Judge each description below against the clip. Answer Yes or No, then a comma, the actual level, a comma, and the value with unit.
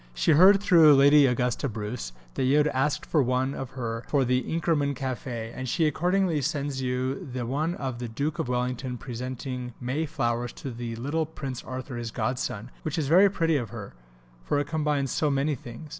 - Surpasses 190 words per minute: Yes, average, 200 wpm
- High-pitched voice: No, low, 135 Hz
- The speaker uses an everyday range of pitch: Yes, average, 3.4 semitones